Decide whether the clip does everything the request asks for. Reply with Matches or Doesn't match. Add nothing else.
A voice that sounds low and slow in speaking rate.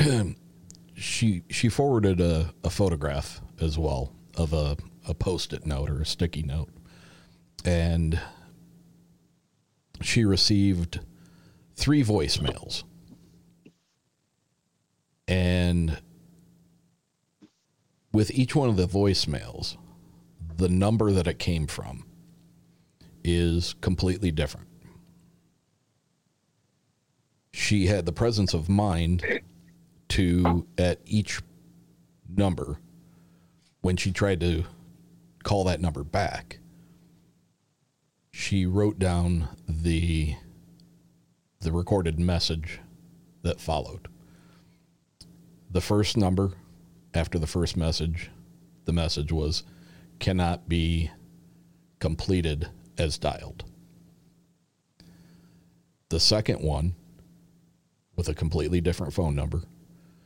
Matches